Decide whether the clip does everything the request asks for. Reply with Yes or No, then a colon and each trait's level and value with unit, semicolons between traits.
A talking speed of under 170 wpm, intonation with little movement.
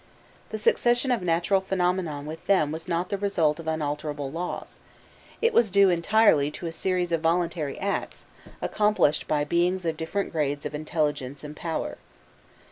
No: average, 160 wpm; average, 3.9 semitones